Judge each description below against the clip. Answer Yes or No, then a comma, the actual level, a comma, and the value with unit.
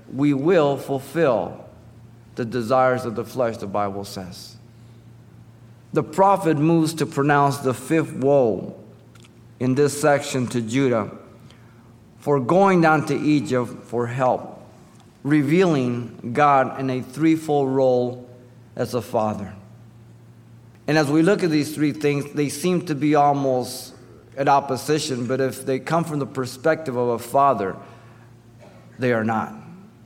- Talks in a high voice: No, low, 130 Hz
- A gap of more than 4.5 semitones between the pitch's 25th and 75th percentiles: No, average, 3.7 semitones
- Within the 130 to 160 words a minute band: Yes, slow, 135 wpm